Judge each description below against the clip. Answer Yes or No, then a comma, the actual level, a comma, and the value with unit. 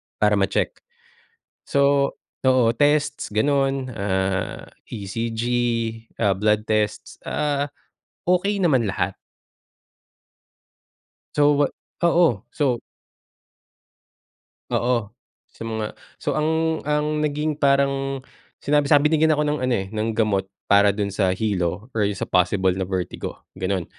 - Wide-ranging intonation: Yes, wide, 6.3 semitones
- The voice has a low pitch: Yes, low, 120 Hz